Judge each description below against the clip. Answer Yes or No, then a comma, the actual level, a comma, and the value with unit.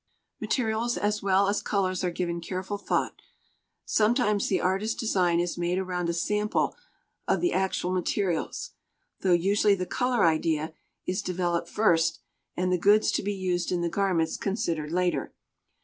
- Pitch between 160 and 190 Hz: Yes, medium, 185 Hz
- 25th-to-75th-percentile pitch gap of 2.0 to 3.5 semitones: Yes, average, 3.0 semitones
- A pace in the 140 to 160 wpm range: Yes, average, 155 wpm